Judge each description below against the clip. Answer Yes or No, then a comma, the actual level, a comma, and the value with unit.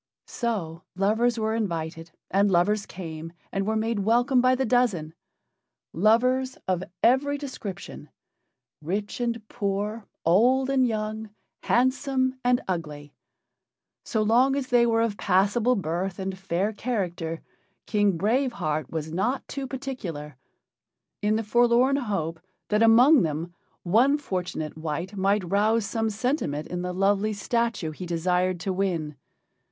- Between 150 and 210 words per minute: No, slow, 135 wpm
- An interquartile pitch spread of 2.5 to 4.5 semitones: No, average, 5.3 semitones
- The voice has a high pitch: Yes, high, 210 Hz